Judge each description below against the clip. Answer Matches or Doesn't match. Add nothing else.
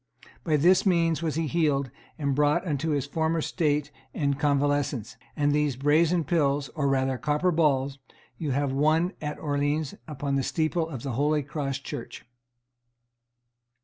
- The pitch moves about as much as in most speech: Doesn't match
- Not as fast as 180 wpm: Matches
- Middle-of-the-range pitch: Matches